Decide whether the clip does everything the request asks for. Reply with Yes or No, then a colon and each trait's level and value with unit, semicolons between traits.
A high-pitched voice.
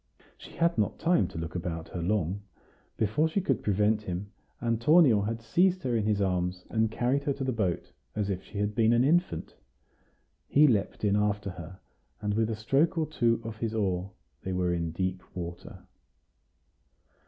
No: low, 105 Hz